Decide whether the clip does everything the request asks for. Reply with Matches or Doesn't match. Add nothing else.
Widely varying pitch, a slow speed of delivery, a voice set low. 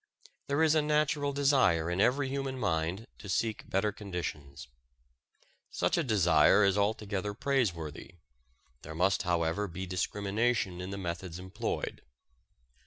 Matches